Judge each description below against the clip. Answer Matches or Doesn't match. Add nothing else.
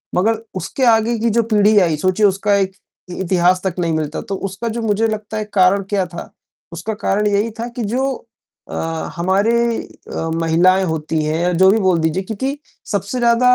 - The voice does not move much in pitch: Doesn't match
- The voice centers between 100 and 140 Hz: Doesn't match